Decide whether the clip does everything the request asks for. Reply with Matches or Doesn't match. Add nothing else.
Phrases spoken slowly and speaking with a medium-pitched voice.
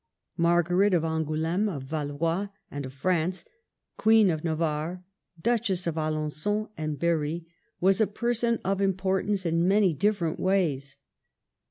Matches